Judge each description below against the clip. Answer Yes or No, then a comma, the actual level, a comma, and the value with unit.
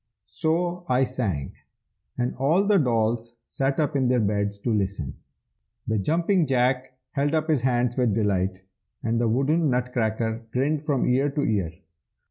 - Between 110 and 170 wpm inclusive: Yes, average, 155 wpm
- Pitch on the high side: No, low, 125 Hz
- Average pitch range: Yes, average, 4.5 semitones